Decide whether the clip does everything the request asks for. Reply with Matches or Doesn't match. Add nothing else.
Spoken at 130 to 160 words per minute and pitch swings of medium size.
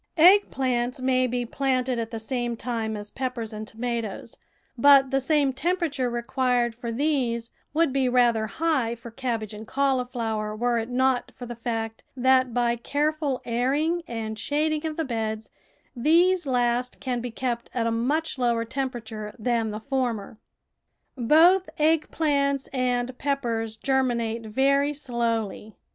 Matches